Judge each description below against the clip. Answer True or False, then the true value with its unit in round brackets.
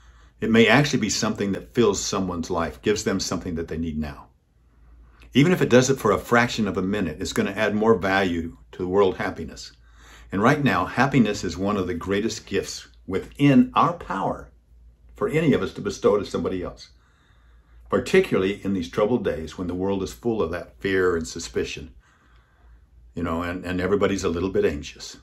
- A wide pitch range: True (7.0 semitones)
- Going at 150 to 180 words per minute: False (195 wpm)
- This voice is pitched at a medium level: False (85 Hz)